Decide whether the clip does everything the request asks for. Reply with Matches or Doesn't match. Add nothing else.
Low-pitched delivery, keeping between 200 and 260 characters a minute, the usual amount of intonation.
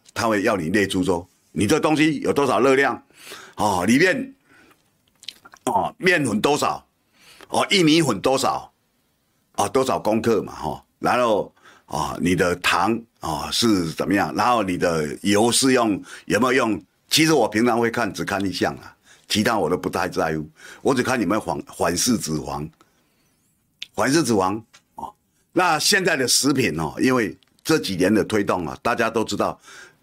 Doesn't match